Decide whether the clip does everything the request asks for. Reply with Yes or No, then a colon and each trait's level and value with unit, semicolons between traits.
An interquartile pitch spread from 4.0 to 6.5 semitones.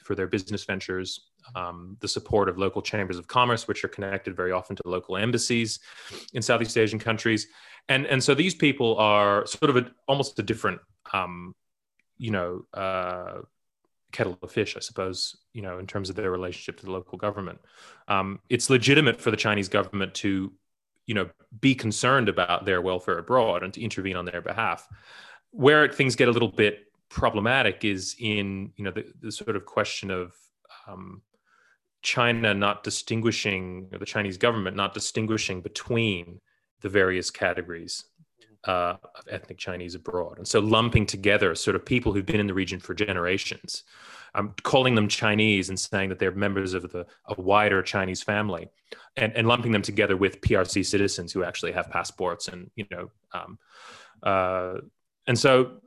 No: average, 3.3 semitones